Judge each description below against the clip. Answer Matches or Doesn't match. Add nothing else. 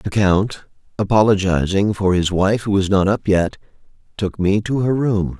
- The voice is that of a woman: Doesn't match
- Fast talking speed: Doesn't match